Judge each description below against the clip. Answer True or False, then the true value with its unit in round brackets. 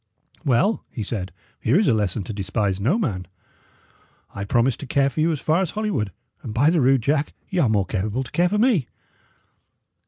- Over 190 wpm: True (205 wpm)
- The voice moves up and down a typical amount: False (7.6 semitones)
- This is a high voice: False (130 Hz)